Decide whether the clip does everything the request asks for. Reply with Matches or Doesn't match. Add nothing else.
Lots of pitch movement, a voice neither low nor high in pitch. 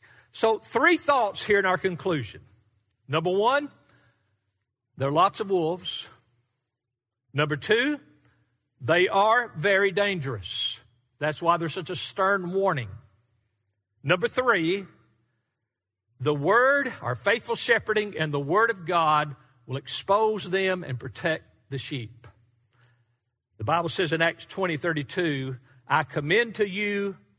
Matches